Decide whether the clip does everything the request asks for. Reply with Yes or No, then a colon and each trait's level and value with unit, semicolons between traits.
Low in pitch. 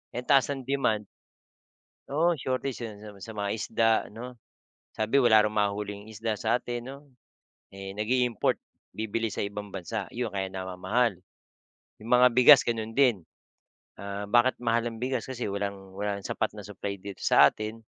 Yes: low, 110 Hz